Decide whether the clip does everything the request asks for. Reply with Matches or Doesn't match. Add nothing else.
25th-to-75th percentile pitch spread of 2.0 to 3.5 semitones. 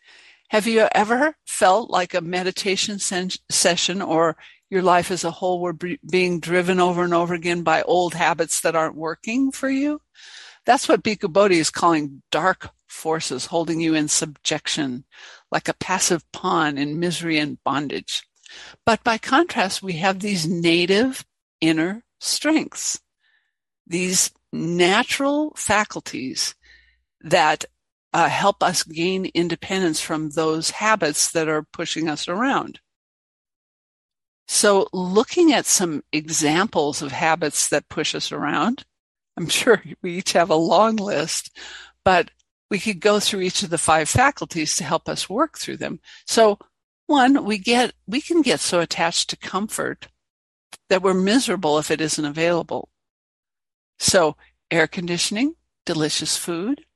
Doesn't match